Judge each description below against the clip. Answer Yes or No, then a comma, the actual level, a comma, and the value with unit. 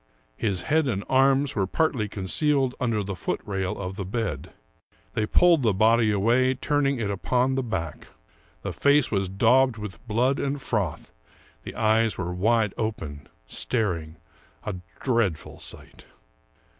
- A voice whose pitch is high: No, low, 110 Hz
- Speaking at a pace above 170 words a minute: No, average, 150 wpm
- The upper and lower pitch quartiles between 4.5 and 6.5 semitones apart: Yes, average, 5.1 semitones